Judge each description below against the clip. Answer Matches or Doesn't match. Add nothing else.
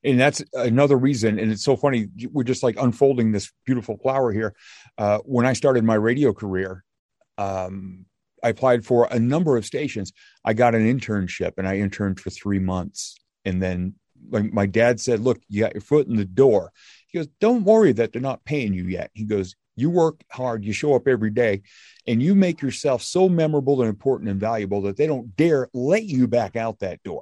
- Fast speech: Matches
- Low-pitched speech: Matches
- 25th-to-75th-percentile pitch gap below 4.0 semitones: Doesn't match